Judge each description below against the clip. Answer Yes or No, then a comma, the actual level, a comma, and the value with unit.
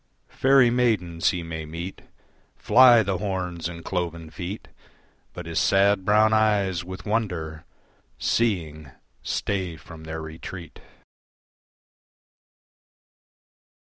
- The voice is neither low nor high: No, very low, 90 Hz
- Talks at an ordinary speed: No, slow, 100 wpm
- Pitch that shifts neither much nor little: Yes, average, 3.9 semitones